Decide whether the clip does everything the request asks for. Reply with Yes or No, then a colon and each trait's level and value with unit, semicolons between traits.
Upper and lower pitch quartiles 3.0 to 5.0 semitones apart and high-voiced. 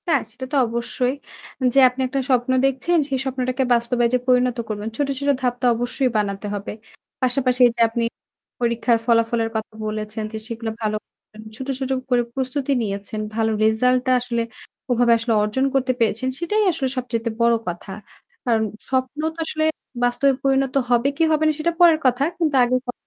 No: narrow, 2.6 semitones; high, 245 Hz